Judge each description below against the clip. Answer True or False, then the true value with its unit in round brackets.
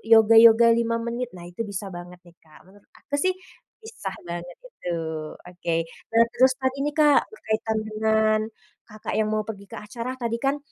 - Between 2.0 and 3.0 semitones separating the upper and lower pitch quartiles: False (3.5 semitones)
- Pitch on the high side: True (220 Hz)